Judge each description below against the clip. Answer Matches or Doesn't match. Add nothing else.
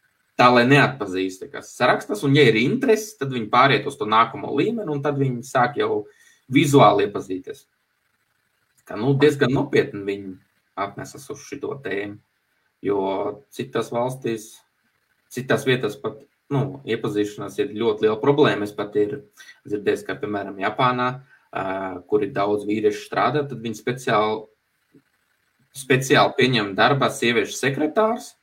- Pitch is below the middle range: Matches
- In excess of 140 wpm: Doesn't match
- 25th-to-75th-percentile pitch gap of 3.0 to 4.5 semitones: Doesn't match